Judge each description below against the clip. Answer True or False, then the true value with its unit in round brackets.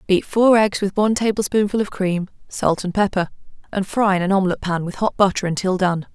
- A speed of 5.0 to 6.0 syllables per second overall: True (5.8 syllables/s)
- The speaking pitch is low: False (195 Hz)